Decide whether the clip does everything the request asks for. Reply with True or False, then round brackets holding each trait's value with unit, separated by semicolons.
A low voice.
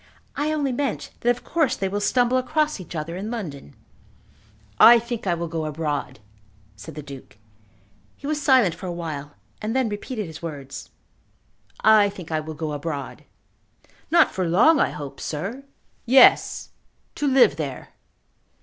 False (190 Hz)